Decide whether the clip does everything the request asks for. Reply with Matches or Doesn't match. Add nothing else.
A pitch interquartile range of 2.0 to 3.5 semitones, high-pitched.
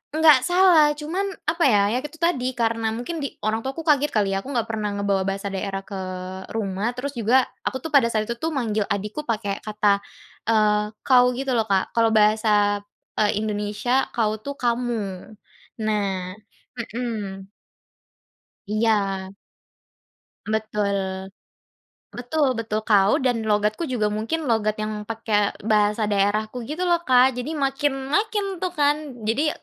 Doesn't match